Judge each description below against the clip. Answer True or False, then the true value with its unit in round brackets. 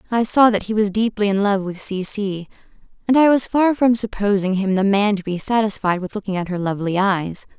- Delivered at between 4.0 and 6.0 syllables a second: True (5.5 syllables/s)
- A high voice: True (205 Hz)